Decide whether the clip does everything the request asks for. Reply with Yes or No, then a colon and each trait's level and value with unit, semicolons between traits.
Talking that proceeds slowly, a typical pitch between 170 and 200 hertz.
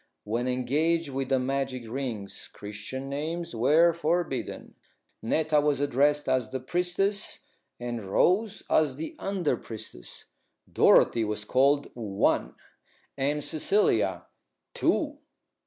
No: slow, 110 wpm; low, 135 Hz